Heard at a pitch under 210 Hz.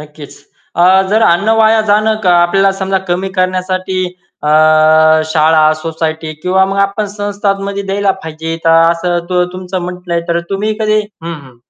Yes: medium, 185 Hz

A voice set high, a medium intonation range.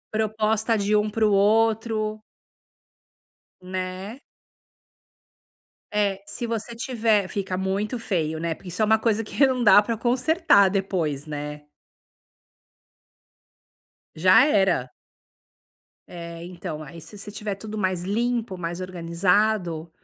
Yes: high, 200 Hz; average, 3.6 semitones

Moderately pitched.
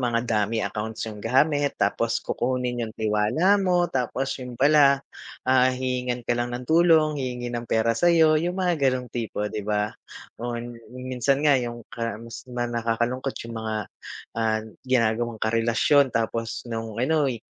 No: low, 120 Hz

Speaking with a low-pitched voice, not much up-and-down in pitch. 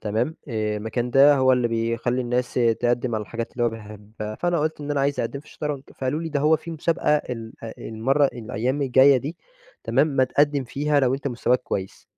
No: low, 130 Hz; average, 3.9 semitones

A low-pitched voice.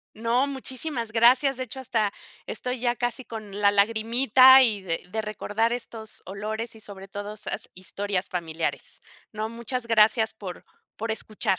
No: high, 220 Hz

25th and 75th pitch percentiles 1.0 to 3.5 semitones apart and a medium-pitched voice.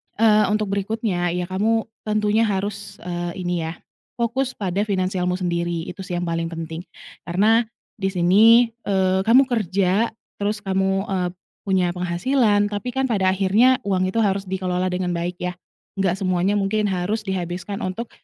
No: average, 3.0 semitones; high, 195 Hz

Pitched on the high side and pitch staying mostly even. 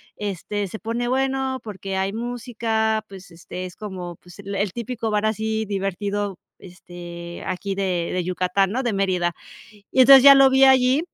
No: high, 205 Hz; average, 4.3 semitones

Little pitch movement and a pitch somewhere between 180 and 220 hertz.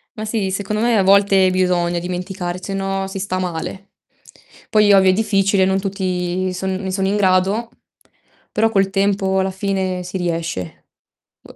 Yes: narrow, 1.3 semitones; high, 190 Hz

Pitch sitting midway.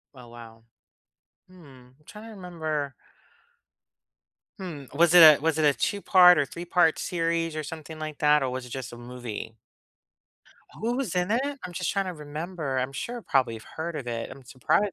Yes: medium, 155 Hz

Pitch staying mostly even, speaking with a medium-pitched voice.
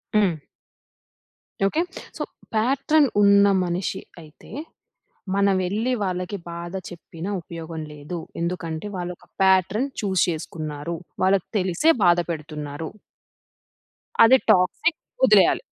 No: average, 3.3 semitones; medium, 180 Hz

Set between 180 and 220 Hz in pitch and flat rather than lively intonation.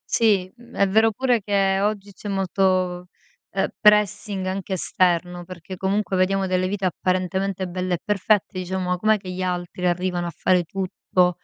Yes: medium, 185 Hz; narrow, 1.6 semitones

